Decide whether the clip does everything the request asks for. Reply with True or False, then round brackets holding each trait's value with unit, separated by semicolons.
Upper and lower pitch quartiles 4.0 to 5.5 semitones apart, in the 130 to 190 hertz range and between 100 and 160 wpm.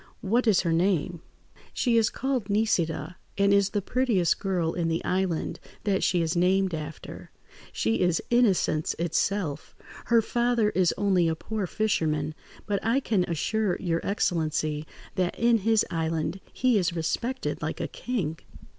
True (4.9 semitones; 185 Hz; 155 wpm)